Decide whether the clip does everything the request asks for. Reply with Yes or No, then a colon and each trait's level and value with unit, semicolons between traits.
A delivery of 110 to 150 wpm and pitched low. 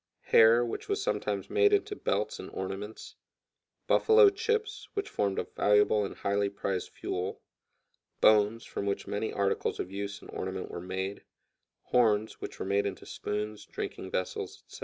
No: average, 160 wpm; low, 105 Hz